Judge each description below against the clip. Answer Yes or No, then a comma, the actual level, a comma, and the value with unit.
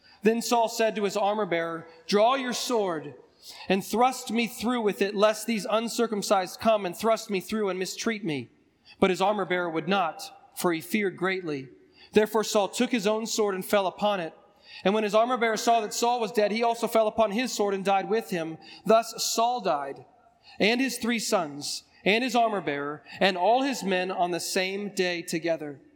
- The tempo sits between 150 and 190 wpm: No, average, 200 wpm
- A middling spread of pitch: Yes, average, 3.6 semitones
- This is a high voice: Yes, high, 210 Hz